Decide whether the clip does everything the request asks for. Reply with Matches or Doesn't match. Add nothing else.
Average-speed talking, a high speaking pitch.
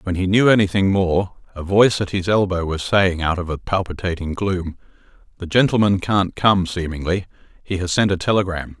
Doesn't match